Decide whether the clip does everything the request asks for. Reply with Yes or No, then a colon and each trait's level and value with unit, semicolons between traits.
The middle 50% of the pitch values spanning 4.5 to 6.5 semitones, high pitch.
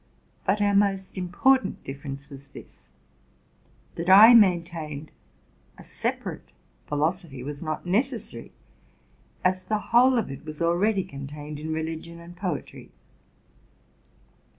No: average, 4.8 semitones; medium, 170 Hz